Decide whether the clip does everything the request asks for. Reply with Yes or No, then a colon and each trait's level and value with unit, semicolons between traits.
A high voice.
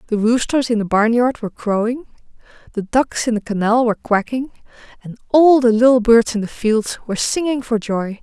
Yes: high, 230 Hz